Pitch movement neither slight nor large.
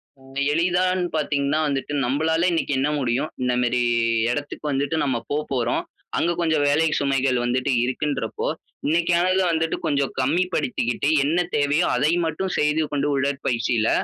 Yes: average, 3.5 semitones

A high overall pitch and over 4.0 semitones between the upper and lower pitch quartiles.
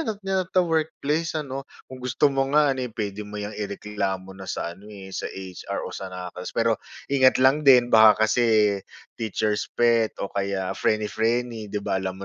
No: low, 110 Hz; average, 4.7 semitones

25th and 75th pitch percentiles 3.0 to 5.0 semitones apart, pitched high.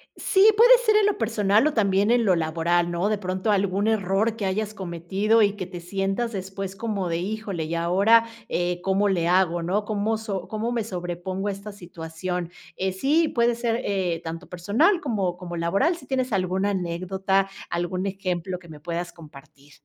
Yes: average, 3.6 semitones; high, 195 Hz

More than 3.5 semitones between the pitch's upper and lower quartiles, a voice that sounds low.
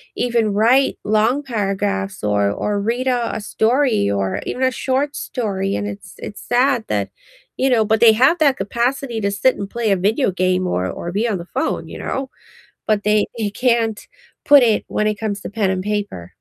No: average, 3.9 semitones; high, 215 Hz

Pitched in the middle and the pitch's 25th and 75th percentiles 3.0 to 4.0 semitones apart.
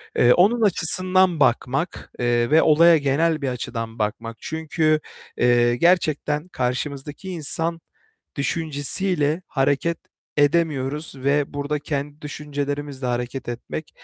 Yes: medium, 145 Hz; average, 3.5 semitones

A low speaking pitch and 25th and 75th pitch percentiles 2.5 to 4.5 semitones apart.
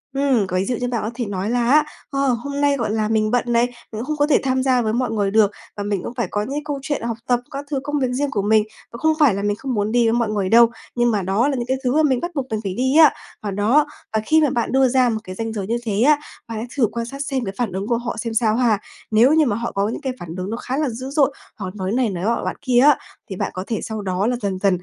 No: high, 235 Hz; average, 4.0 semitones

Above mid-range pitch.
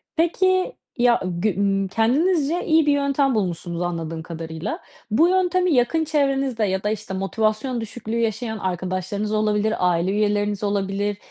Yes: high, 215 Hz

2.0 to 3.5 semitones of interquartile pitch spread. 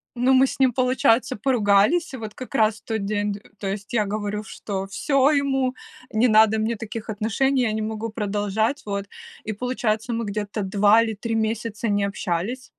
Yes: average, 3.2 semitones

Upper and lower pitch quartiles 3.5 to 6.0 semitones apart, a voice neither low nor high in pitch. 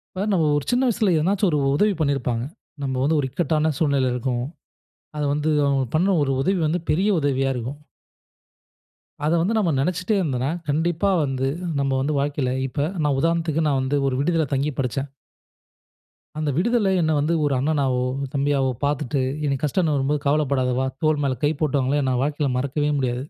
No: average, 3.0 semitones; medium, 145 Hz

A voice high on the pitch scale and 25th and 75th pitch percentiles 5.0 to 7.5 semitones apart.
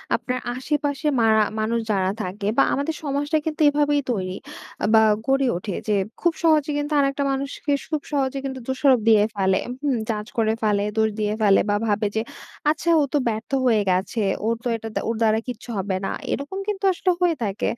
Yes: high, 245 Hz; average, 5.3 semitones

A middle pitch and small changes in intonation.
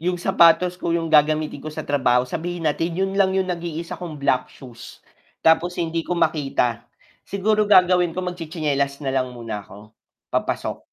No: medium, 165 Hz; average, 4.2 semitones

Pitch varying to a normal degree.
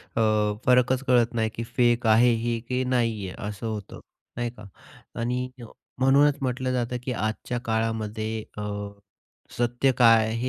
No: narrow, 2.1 semitones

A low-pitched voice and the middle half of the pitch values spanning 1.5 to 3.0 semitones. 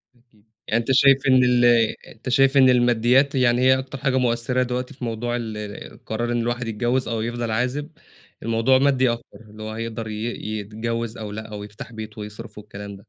Yes: low, 120 Hz; narrow, 2.5 semitones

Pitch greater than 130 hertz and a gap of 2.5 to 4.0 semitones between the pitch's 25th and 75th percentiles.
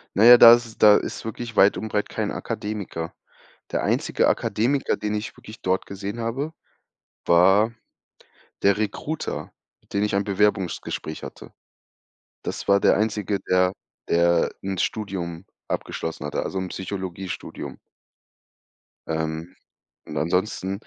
No: low, 100 Hz; average, 2.8 semitones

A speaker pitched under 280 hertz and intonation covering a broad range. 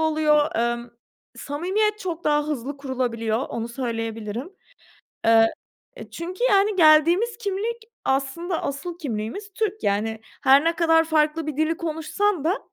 No: very high, 310 Hz; wide, 6.5 semitones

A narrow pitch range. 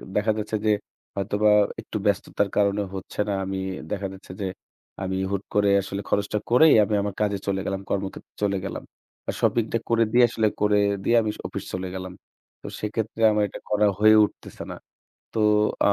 Yes: narrow, 1.6 semitones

